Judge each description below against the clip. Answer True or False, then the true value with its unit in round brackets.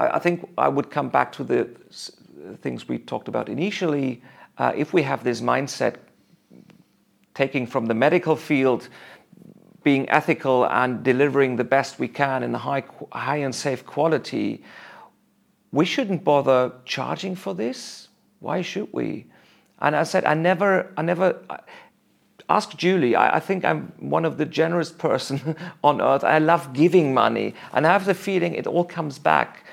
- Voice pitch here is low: False (150 Hz)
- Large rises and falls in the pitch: False (4.5 semitones)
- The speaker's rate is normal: True (165 wpm)